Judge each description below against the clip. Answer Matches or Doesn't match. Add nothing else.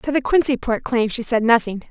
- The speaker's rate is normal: Doesn't match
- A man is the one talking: Doesn't match